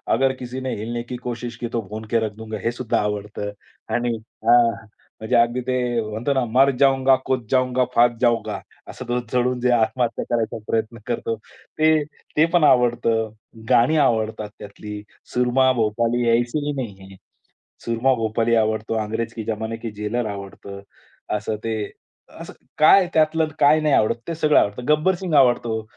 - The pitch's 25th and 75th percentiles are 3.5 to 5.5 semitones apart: No, average, 2.7 semitones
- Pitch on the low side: Yes, low, 120 Hz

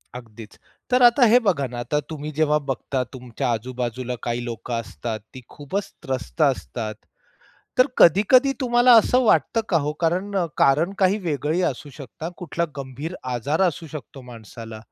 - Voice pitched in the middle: Yes, medium, 145 Hz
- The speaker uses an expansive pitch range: Yes, wide, 6.8 semitones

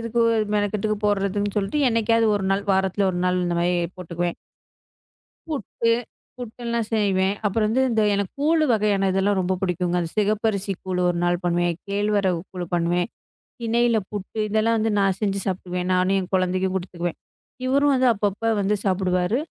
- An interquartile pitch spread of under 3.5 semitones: Yes, average, 3.1 semitones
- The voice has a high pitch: Yes, high, 200 Hz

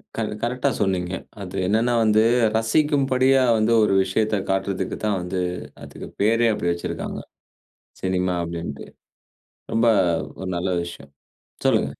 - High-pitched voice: No, low, 100 Hz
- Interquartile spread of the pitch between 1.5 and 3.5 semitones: No, average, 3.9 semitones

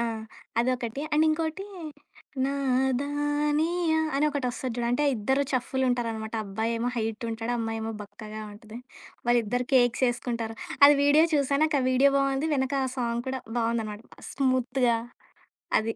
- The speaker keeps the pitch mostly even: No, average, 3.5 semitones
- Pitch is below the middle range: No, very high, 250 Hz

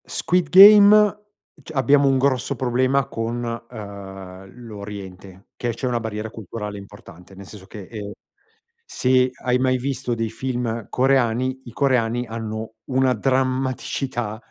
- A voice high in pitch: No, low, 120 Hz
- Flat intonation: No, average, 3.8 semitones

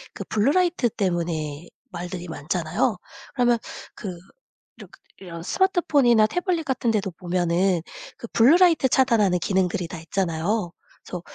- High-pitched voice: Yes, high, 195 Hz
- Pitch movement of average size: No, wide, 6.0 semitones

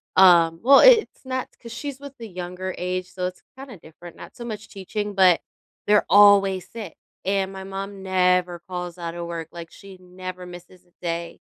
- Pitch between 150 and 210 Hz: Yes, medium, 185 Hz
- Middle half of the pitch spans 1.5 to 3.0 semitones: Yes, narrow, 2.5 semitones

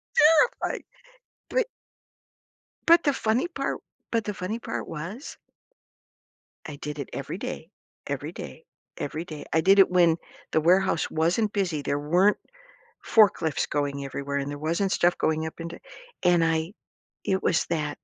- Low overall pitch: No, medium, 170 Hz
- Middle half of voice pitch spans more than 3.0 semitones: Yes, average, 4.8 semitones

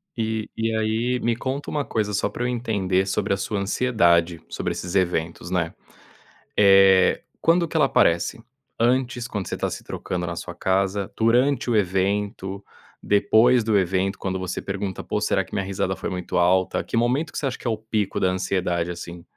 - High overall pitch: No, low, 100 Hz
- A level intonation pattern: No, average, 3.8 semitones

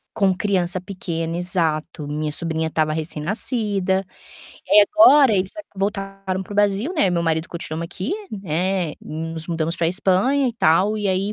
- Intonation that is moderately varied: Yes, average, 3.6 semitones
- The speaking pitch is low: No, medium, 185 Hz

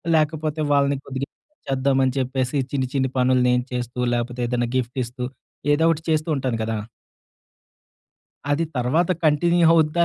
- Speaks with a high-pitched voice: No, low, 135 Hz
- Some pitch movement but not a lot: Yes, average, 3.6 semitones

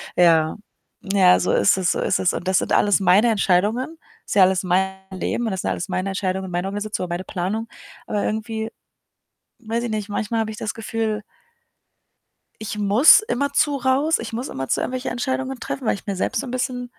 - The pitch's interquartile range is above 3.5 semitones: Yes, average, 4.2 semitones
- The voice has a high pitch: Yes, high, 210 Hz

